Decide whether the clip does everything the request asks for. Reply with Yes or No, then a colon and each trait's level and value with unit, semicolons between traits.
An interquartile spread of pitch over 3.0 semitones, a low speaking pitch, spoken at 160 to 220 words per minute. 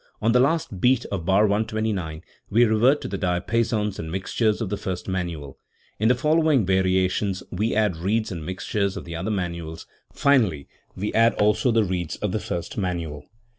Yes: average, 3.8 semitones; low, 100 Hz; average, 180 wpm